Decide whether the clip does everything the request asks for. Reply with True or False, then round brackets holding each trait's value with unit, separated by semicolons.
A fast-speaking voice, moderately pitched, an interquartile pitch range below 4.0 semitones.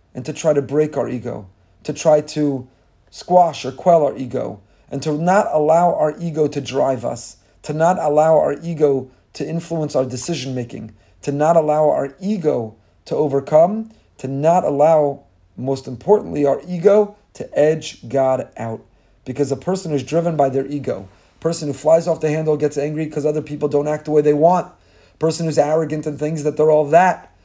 False (190 wpm; 150 Hz; 3.2 semitones)